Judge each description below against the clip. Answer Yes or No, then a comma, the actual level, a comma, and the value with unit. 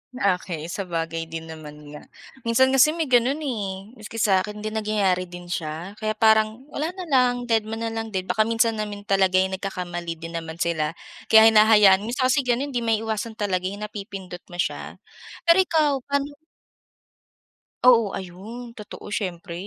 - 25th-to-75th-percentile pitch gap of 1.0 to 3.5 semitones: No, average, 4.1 semitones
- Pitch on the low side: No, high, 210 Hz